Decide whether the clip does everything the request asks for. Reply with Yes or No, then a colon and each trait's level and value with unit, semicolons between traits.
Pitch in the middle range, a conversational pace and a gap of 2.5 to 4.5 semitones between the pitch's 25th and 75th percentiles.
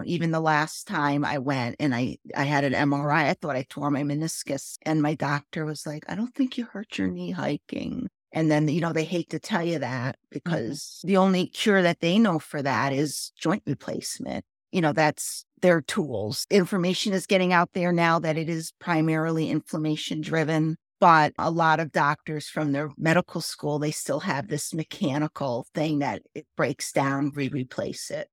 Yes: medium, 155 Hz; average, 195 wpm; average, 2.8 semitones